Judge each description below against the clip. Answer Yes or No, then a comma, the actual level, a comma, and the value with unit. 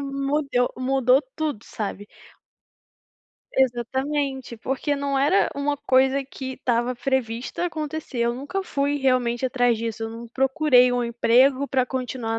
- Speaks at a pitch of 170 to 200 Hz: No, very high, 260 Hz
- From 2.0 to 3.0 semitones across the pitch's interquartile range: Yes, narrow, 2.5 semitones